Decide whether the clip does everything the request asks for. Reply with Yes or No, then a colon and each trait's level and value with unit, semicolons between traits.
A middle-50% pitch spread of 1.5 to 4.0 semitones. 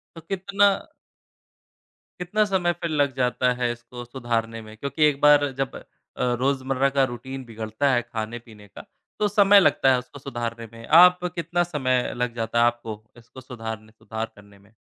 No: average, 4.4 semitones